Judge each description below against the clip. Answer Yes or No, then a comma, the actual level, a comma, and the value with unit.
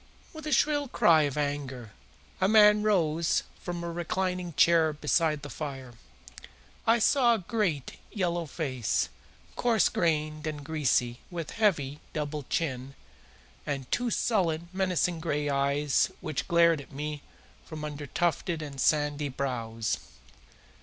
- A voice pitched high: No, medium, 155 Hz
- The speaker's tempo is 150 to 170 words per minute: No, slow, 135 wpm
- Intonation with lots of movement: No, average, 3.8 semitones